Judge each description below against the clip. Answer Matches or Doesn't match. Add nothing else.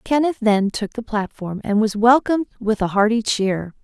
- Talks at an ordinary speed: Matches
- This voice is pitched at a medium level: Doesn't match